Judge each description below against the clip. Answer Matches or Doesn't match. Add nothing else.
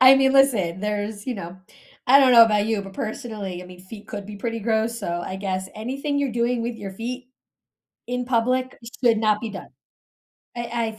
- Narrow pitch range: Doesn't match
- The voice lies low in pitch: Doesn't match